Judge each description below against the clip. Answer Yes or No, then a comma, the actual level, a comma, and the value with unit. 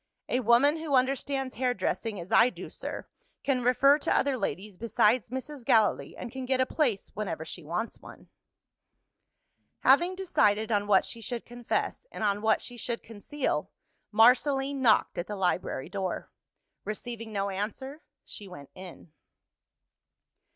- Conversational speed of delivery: Yes, average, 150 wpm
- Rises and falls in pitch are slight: No, average, 4.4 semitones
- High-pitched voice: Yes, high, 235 Hz